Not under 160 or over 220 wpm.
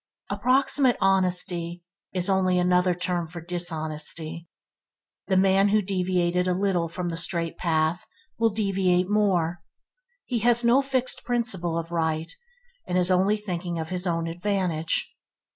No: average, 140 wpm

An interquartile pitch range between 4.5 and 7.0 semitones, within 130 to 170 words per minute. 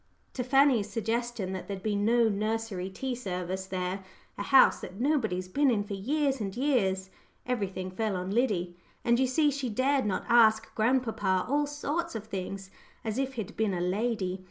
No: average, 4.9 semitones; average, 185 wpm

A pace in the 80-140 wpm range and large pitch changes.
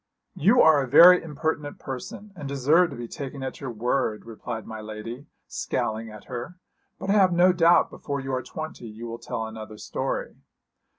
No: average, 185 wpm; wide, 5.9 semitones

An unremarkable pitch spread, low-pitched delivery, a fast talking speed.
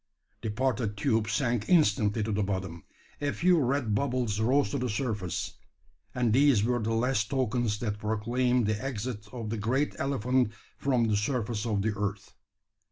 No: average, 3.4 semitones; low, 115 Hz; average, 165 wpm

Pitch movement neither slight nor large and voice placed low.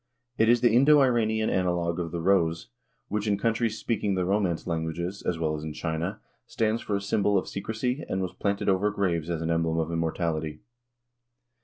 Yes: average, 4.6 semitones; very low, 95 Hz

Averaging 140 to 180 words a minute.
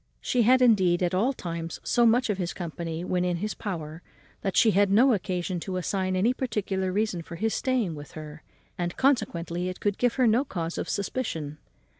No: average, 200 wpm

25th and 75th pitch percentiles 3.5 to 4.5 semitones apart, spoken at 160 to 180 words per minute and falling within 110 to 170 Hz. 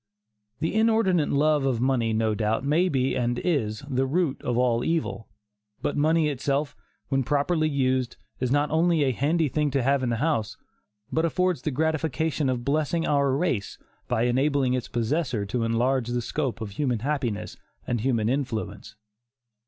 Yes: average, 4.1 semitones; average, 170 wpm; low, 135 Hz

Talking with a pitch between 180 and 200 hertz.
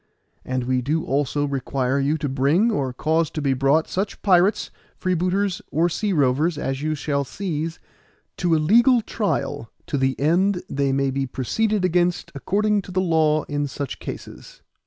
No: medium, 155 Hz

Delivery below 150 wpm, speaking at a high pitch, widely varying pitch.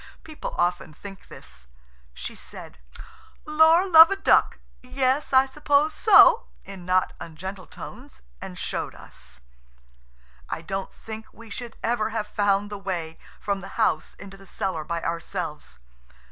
Yes: average, 140 wpm; high, 200 Hz; wide, 6.9 semitones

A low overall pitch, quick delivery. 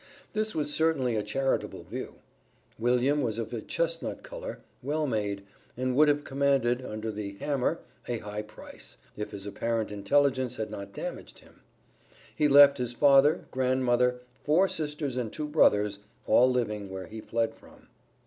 No: low, 125 Hz; average, 160 wpm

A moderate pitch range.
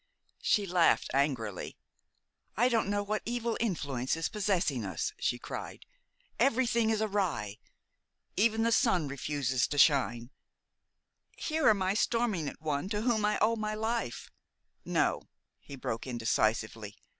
No: wide, 8.9 semitones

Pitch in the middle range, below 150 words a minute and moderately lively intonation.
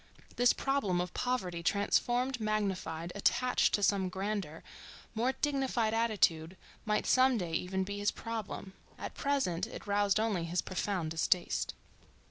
No: high, 205 Hz; slow, 135 wpm; average, 4.7 semitones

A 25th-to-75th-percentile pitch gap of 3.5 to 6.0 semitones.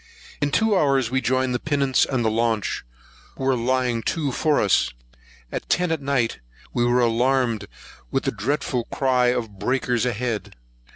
No: narrow, 2.6 semitones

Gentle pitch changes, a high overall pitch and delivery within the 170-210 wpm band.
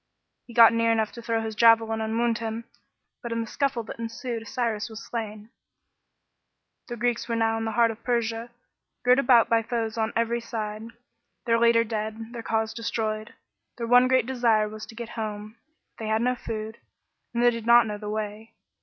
Yes: narrow, 1.2 semitones; high, 230 Hz; average, 200 wpm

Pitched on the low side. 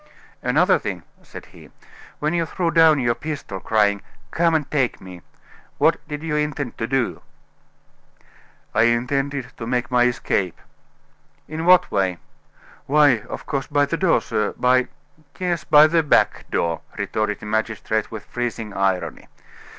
Yes: low, 130 Hz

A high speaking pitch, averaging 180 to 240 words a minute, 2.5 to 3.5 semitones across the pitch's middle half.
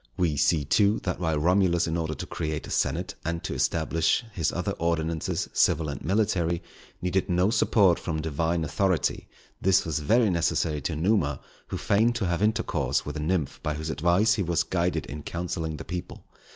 No: very low, 85 Hz; average, 185 wpm; average, 3.1 semitones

